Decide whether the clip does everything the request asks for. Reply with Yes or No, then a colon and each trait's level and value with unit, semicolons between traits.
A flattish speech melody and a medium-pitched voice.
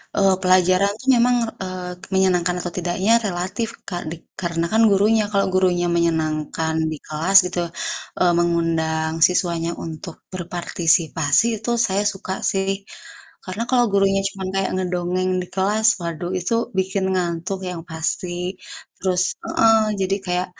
Yes: narrow, 2.2 semitones; medium, 180 Hz